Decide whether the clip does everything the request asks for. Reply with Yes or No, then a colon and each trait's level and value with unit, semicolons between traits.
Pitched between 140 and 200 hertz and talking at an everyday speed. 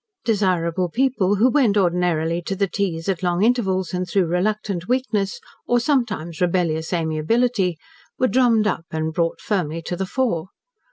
Yes: medium, 185 Hz; average, 155 wpm